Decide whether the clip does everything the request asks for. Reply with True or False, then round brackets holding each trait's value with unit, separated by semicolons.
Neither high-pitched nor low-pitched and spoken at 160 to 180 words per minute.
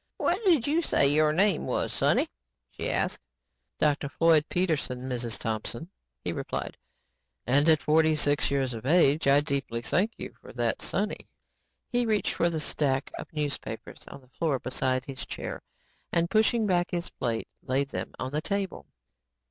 True (150 Hz; 165 wpm)